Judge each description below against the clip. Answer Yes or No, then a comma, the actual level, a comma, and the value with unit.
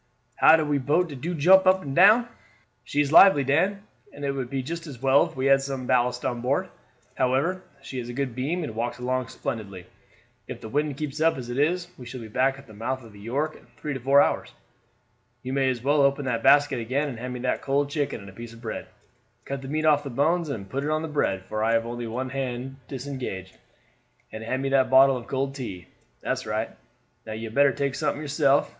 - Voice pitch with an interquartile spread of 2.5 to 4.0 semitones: Yes, average, 3.1 semitones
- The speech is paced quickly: Yes, fast, 235 wpm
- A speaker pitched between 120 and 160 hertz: Yes, low, 135 Hz